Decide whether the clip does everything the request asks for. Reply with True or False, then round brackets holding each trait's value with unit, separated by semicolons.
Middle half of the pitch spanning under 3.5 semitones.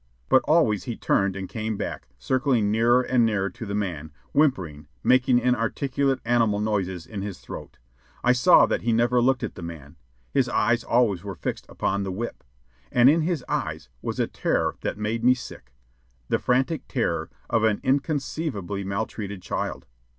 False (4.3 semitones)